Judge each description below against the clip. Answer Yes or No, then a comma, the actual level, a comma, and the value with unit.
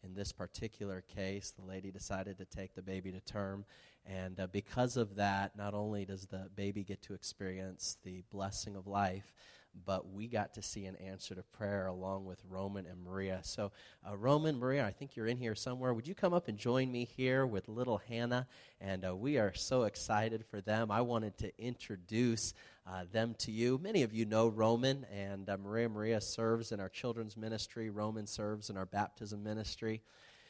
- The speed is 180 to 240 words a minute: Yes, average, 200 wpm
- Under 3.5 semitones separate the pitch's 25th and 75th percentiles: Yes, average, 3.0 semitones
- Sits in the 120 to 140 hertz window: No, low, 105 Hz